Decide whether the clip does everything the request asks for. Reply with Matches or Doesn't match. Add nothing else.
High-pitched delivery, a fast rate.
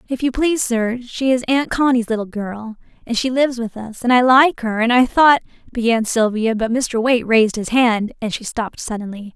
Matches